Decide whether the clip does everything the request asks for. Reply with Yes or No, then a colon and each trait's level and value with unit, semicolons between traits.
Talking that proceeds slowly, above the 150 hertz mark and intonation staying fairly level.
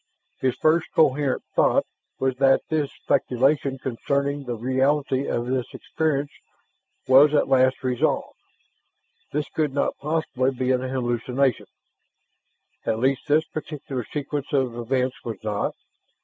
No: slow, 125 wpm; low, 135 Hz; narrow, 2.1 semitones